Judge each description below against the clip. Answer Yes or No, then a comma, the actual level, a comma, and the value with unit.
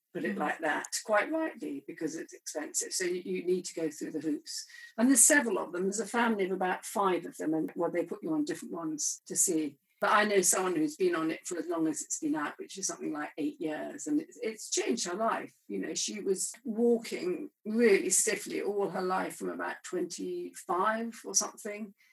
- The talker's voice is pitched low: No, high, 235 Hz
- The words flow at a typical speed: No, fast, 220 wpm